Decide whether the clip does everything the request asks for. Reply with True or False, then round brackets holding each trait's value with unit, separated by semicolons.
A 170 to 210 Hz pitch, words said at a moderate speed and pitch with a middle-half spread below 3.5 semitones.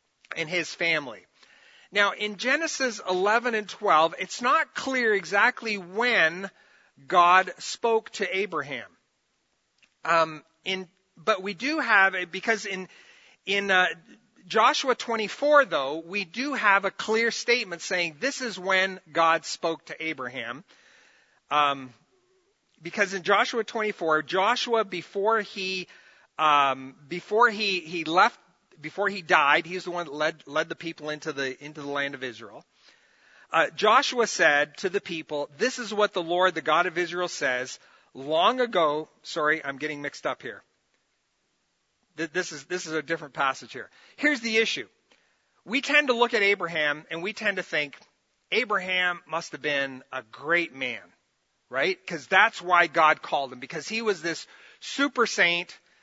False (185 Hz; 155 wpm; 5.6 semitones)